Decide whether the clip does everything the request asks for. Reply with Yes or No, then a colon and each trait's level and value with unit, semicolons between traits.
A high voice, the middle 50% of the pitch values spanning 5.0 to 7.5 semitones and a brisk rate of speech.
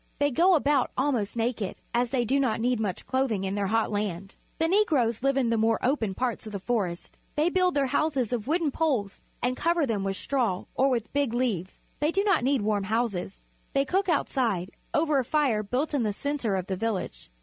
Yes: high, 245 Hz; wide, 5.4 semitones; fast, 215 wpm